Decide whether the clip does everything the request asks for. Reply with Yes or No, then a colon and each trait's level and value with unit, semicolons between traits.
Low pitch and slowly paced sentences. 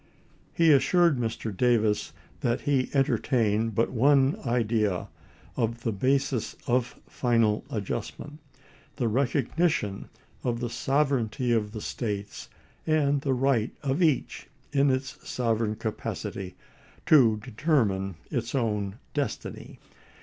Yes: low, 120 Hz; slow, 120 wpm